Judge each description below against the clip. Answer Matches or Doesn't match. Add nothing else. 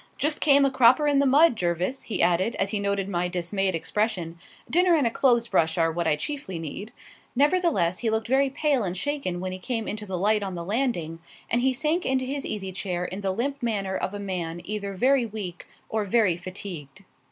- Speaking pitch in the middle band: Doesn't match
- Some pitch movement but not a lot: Doesn't match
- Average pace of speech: Doesn't match